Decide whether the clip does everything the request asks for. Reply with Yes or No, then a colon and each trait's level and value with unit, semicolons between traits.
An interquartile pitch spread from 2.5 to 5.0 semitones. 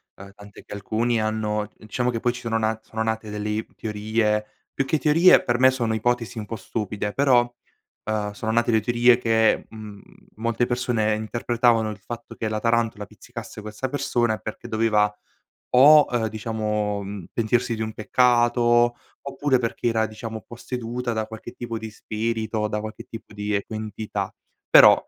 No: narrow, 1.9 semitones